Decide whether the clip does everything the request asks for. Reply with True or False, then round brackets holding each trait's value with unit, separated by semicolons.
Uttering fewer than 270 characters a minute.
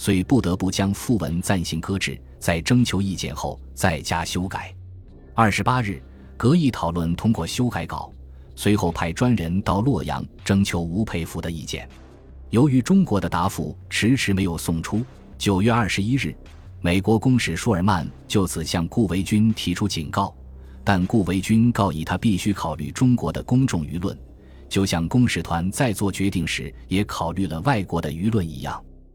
True (260 characters per minute)